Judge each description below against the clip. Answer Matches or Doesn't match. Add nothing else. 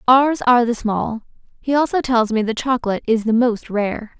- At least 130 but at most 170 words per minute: Doesn't match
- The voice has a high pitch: Matches